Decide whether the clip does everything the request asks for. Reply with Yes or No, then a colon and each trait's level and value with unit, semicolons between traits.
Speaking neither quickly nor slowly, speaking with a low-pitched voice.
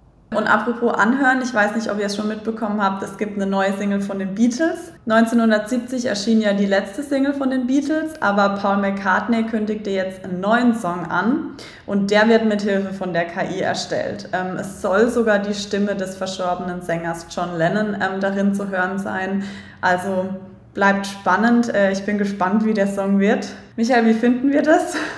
No: average, 180 wpm; high, 205 Hz